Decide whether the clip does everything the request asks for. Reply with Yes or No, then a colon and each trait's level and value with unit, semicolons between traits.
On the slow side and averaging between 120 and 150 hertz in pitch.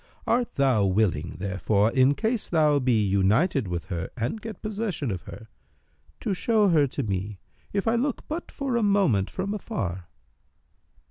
No: average, 160 wpm; low, 135 Hz